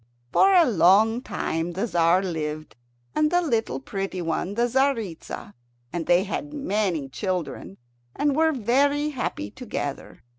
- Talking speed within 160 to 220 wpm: No, average, 140 wpm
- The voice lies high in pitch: Yes, high, 200 Hz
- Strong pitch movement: Yes, wide, 8.4 semitones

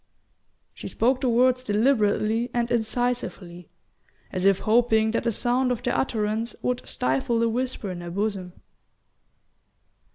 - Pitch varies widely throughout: No, average, 3.1 semitones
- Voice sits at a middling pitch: No, high, 230 Hz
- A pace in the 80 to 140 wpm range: Yes, slow, 135 wpm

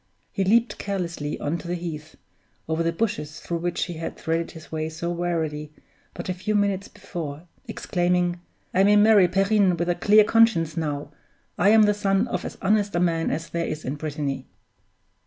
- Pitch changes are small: No, average, 3.8 semitones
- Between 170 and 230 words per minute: Yes, average, 190 wpm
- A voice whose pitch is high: No, medium, 175 Hz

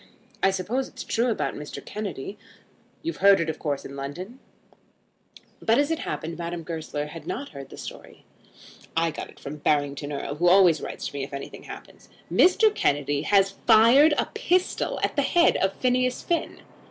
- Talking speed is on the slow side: No, average, 185 wpm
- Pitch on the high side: No, medium, 180 Hz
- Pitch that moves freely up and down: Yes, wide, 8.5 semitones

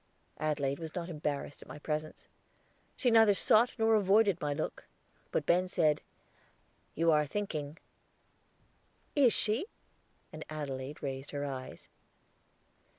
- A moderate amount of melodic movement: No, wide, 5.9 semitones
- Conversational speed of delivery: No, slow, 125 wpm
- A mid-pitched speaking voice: Yes, medium, 155 Hz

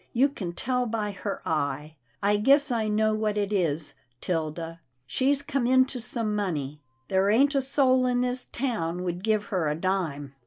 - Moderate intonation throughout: No, wide, 6.8 semitones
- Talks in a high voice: Yes, high, 210 Hz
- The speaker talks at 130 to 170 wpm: No, average, 180 wpm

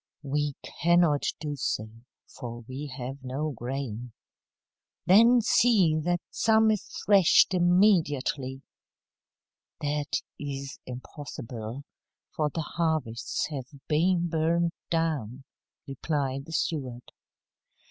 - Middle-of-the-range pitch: Yes, medium, 145 Hz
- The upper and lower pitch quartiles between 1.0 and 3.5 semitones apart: No, average, 4.5 semitones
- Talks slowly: Yes, slow, 95 wpm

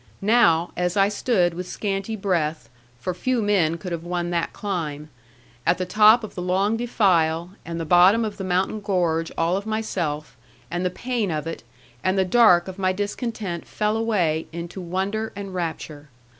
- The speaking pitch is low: No, medium, 185 Hz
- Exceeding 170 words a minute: Yes, average, 180 wpm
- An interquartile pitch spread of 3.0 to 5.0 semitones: Yes, average, 3.5 semitones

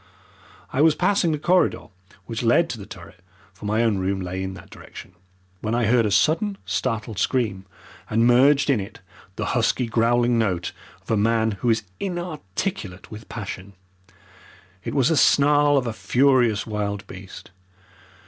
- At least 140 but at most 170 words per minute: Yes, average, 165 wpm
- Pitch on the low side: Yes, low, 115 Hz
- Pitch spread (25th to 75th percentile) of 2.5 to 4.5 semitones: No, wide, 5.5 semitones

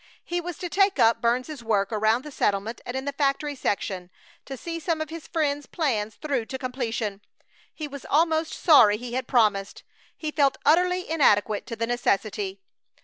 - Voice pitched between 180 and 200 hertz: No, very high, 265 Hz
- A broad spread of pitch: Yes, wide, 5.8 semitones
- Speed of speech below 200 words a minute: Yes, average, 180 wpm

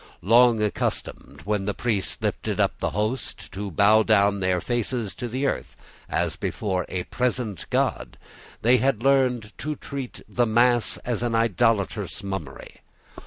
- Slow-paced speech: No, average, 155 wpm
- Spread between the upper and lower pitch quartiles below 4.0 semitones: Yes, average, 3.4 semitones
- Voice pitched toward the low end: Yes, low, 110 Hz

